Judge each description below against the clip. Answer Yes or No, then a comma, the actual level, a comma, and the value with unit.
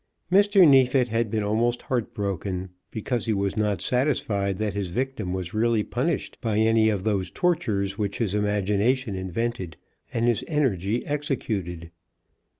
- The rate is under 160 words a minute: Yes, average, 150 wpm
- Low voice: Yes, low, 110 Hz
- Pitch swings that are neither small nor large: Yes, average, 3.9 semitones